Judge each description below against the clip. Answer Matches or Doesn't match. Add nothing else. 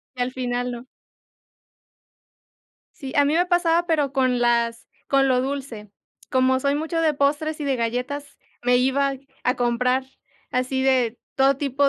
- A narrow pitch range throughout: Matches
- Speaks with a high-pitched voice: Matches